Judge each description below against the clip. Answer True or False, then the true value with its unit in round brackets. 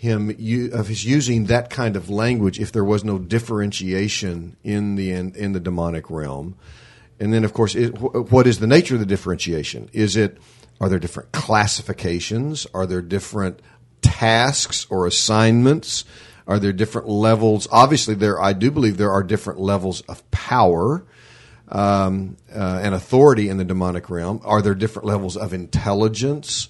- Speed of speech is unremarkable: True (165 wpm)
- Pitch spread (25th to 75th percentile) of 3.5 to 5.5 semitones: False (3.1 semitones)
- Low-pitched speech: True (105 Hz)